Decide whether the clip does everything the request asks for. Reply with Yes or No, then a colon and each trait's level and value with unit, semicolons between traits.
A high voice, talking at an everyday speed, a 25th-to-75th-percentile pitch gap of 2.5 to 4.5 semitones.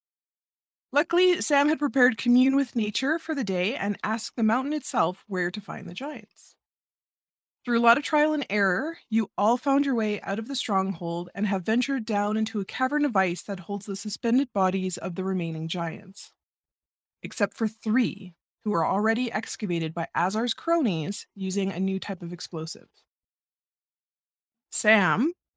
No: high, 215 Hz; average, 165 wpm; average, 5.2 semitones